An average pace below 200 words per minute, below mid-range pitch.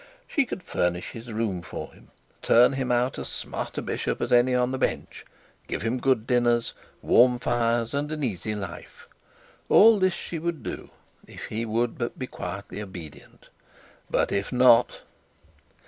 Yes: average, 165 wpm; low, 120 Hz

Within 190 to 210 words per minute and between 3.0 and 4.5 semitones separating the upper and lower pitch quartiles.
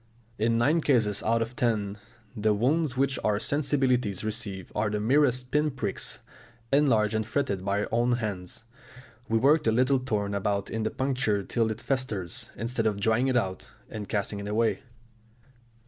No: average, 170 wpm; average, 3.7 semitones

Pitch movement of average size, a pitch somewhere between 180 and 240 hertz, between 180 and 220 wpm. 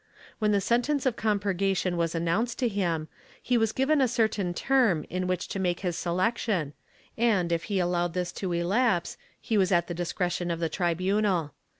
Yes: average, 4.1 semitones; medium, 185 Hz; average, 185 wpm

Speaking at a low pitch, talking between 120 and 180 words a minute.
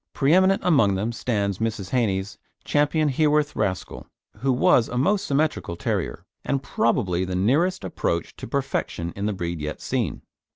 Yes: low, 120 Hz; average, 155 wpm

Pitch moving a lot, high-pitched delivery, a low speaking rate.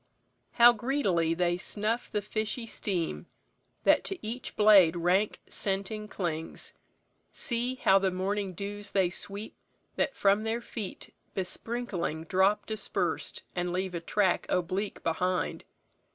No: average, 3.2 semitones; high, 200 Hz; slow, 125 wpm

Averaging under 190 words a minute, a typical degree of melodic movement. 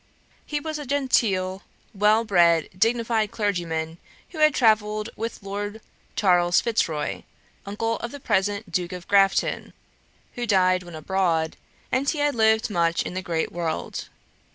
Yes: average, 140 wpm; average, 4.4 semitones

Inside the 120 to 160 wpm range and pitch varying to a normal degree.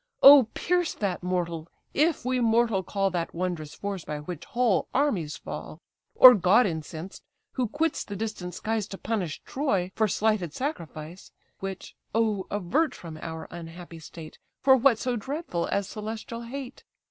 No: average, 155 wpm; wide, 6.0 semitones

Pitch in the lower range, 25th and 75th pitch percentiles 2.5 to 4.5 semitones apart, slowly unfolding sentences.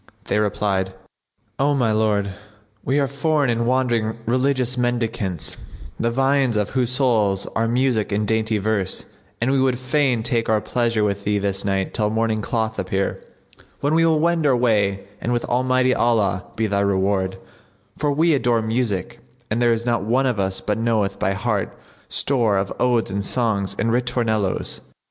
No: low, 115 Hz; average, 3.8 semitones; average, 170 wpm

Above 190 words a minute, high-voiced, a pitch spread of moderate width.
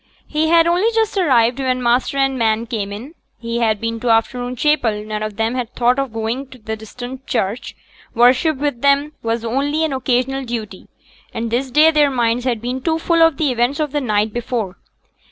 Yes: fast, 205 wpm; very high, 250 Hz; average, 3.6 semitones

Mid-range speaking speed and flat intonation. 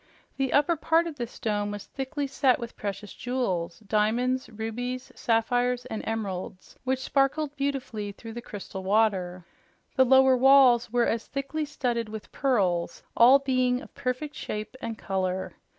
No: average, 150 wpm; average, 4.0 semitones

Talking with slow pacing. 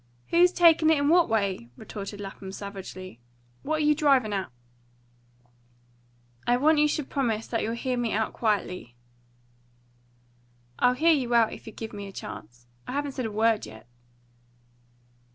No: average, 155 wpm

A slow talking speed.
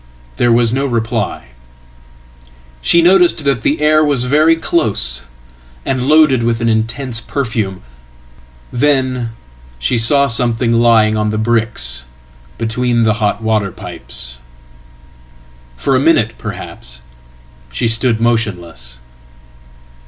Yes: slow, 105 wpm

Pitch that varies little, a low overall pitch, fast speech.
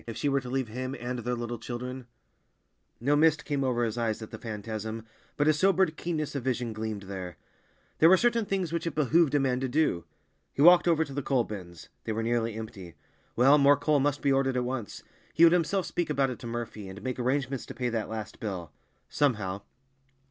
No: average, 4.6 semitones; low, 125 Hz; fast, 215 wpm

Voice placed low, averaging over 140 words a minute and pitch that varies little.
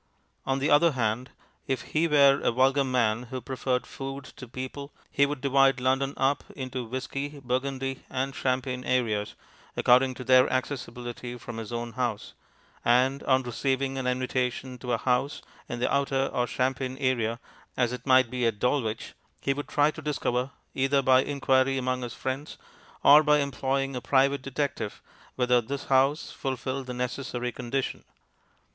Yes: low, 130 Hz; average, 165 wpm; narrow, 1.7 semitones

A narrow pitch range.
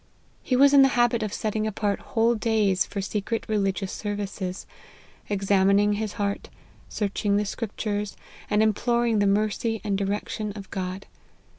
Yes: narrow, 1.9 semitones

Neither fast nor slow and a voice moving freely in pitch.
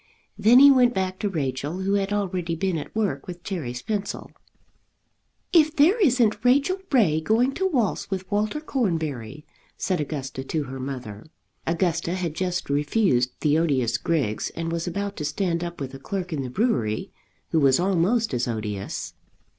Yes: average, 170 wpm; wide, 6.8 semitones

